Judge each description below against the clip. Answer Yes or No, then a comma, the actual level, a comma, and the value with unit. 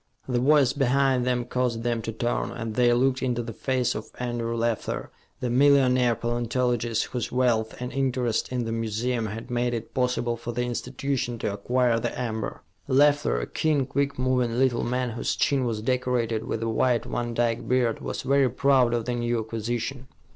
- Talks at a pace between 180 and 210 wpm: Yes, average, 185 wpm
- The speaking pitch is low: Yes, low, 120 Hz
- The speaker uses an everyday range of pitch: No, narrow, 1.7 semitones